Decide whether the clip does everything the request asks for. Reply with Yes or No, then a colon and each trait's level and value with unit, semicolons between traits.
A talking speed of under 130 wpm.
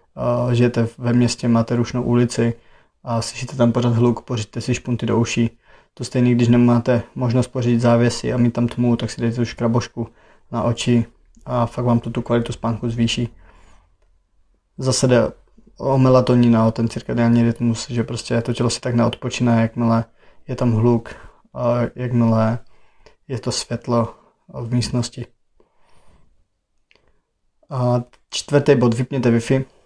No: average, 145 wpm